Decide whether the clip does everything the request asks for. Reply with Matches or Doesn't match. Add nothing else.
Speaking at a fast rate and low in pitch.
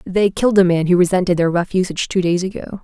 Doesn't match